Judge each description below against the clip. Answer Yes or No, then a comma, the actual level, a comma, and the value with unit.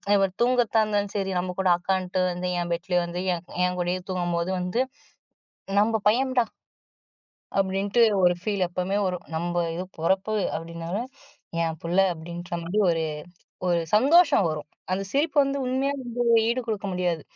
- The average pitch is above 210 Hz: No, medium, 185 Hz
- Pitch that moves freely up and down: No, average, 4.0 semitones